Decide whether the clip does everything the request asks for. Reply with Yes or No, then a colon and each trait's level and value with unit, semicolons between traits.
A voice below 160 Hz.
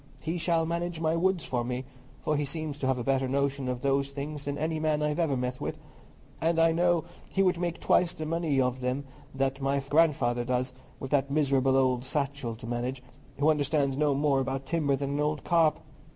Yes: medium, 140 Hz